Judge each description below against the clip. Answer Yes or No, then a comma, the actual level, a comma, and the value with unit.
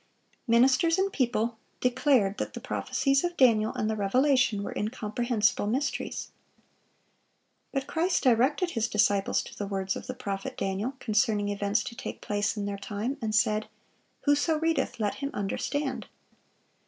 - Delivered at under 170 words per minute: Yes, average, 150 wpm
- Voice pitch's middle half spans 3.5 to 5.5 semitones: Yes, average, 4.7 semitones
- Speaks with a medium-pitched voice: No, high, 230 Hz